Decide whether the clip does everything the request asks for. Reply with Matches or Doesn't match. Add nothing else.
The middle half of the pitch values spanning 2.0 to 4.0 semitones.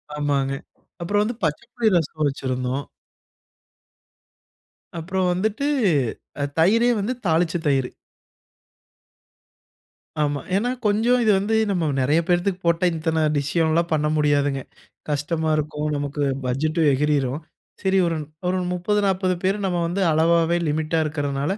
Doesn't match